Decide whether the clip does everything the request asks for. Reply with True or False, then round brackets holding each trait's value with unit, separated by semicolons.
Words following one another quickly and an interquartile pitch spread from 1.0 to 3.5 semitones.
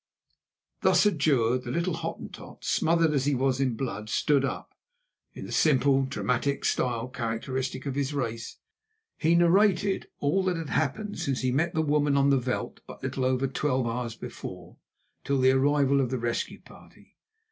False (170 wpm; 3.1 semitones)